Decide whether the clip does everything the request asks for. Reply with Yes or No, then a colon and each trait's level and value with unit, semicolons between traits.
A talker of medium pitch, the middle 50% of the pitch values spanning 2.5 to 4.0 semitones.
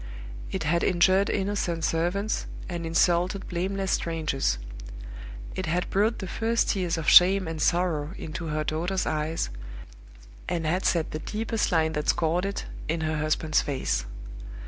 Yes: medium, 170 Hz; average, 3.3 semitones